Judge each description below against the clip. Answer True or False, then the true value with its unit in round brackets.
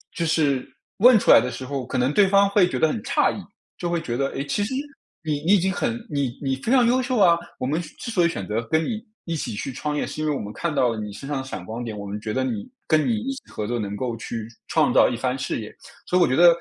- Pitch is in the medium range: True (145 Hz)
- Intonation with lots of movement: True (7.2 semitones)